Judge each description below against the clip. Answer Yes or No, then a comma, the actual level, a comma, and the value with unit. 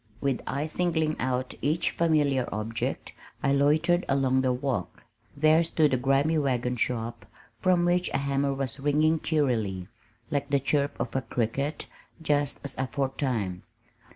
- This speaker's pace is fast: No, average, 145 wpm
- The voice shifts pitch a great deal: No, average, 3.3 semitones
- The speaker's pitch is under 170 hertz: Yes, medium, 140 Hz